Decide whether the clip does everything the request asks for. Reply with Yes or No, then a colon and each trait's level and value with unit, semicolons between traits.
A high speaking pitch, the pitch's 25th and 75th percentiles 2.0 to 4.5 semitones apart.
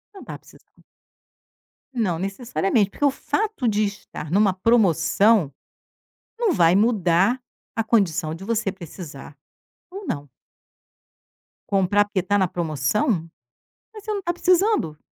No: high, 200 Hz; wide, 5.6 semitones